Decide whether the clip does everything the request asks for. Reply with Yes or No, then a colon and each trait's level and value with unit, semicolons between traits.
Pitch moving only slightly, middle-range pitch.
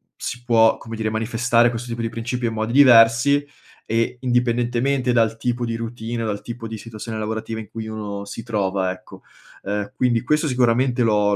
No: narrow, 1.7 semitones; low, 115 Hz